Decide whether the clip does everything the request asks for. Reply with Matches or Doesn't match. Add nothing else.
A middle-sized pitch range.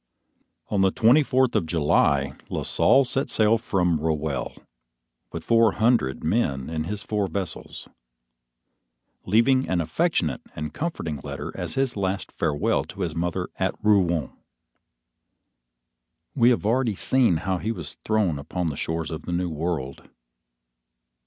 Doesn't match